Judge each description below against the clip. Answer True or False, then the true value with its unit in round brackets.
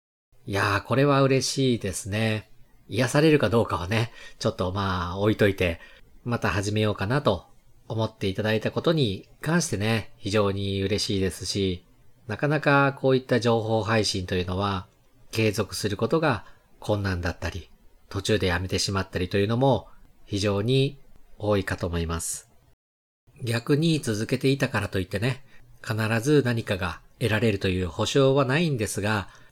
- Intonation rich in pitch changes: False (4.4 semitones)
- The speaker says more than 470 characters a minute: False (325 characters per minute)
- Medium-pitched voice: False (110 Hz)